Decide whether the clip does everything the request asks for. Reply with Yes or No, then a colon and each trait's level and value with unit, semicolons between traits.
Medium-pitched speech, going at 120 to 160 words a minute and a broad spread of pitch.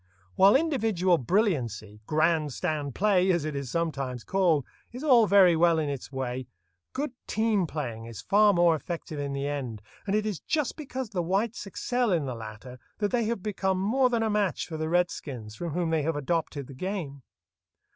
No: medium, 170 Hz; average, 185 wpm; wide, 6.6 semitones